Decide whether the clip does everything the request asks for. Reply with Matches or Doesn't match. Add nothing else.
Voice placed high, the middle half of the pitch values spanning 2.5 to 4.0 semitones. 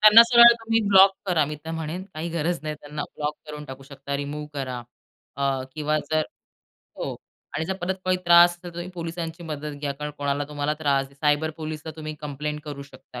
Doesn't match